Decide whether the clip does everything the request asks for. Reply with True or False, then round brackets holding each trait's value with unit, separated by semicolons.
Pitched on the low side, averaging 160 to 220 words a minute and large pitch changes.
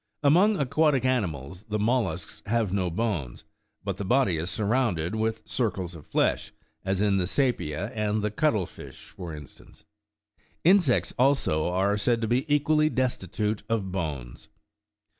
False (105 Hz; 145 wpm; 6.2 semitones)